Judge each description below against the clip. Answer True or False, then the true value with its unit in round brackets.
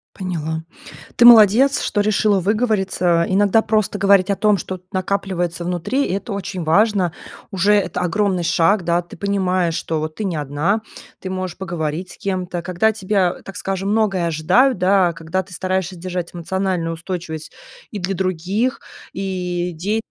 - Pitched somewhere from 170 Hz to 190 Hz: True (185 Hz)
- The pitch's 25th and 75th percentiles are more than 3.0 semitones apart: False (2.5 semitones)